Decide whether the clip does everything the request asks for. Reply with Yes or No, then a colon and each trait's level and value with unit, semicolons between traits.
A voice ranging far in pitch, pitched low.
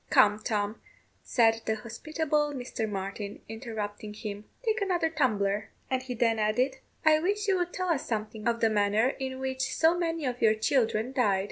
No: wide, 5.7 semitones; high, 235 Hz